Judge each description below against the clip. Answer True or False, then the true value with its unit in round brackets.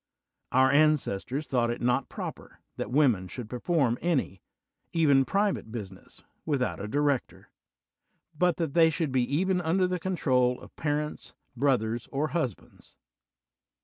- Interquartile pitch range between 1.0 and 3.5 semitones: False (4.7 semitones)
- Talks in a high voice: False (140 Hz)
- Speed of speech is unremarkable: True (160 wpm)